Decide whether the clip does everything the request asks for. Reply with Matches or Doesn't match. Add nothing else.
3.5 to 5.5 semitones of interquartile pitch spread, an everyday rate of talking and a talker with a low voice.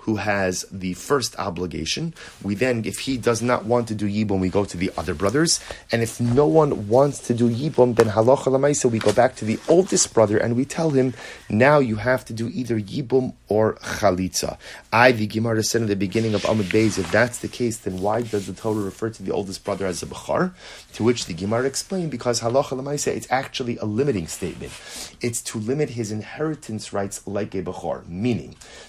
Doesn't match